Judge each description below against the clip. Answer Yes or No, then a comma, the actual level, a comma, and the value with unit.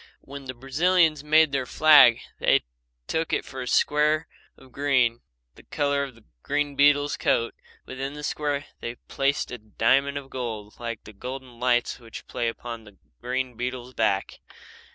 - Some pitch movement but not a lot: Yes, average, 3.2 semitones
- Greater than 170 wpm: No, average, 165 wpm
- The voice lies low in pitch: Yes, low, 130 Hz